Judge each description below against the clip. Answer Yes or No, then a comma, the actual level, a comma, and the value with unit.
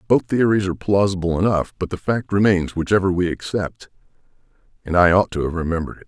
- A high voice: No, very low, 95 Hz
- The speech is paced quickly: No, average, 190 wpm